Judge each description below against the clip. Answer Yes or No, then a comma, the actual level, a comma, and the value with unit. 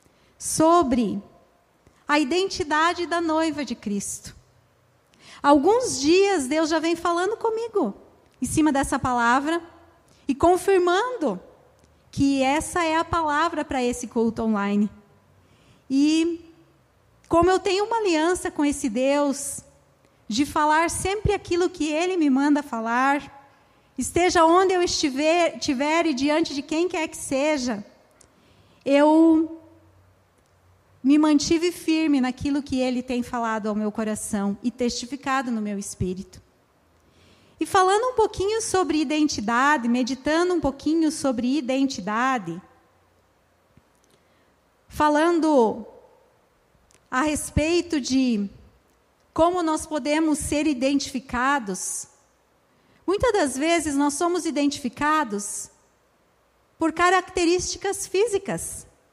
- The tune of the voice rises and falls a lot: No, average, 4.6 semitones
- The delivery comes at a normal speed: No, slow, 105 wpm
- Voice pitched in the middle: No, very high, 300 Hz